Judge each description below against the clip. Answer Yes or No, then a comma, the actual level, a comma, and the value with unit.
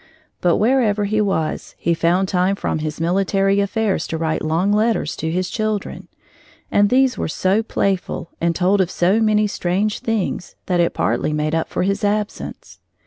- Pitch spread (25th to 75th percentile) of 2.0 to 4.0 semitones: Yes, average, 3.6 semitones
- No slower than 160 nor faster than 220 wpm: Yes, average, 175 wpm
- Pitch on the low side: No, high, 195 Hz